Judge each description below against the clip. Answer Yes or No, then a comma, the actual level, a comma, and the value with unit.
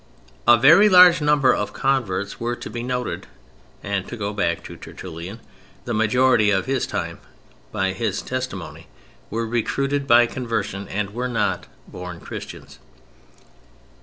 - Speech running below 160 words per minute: Yes, average, 140 wpm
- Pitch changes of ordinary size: Yes, average, 4.3 semitones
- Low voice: Yes, low, 115 Hz